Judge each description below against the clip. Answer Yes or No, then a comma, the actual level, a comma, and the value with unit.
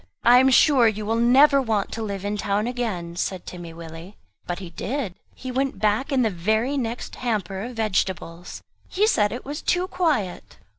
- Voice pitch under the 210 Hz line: No, high, 220 Hz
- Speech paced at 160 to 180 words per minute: No, average, 190 wpm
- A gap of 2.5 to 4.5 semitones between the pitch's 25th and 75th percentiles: No, average, 5.1 semitones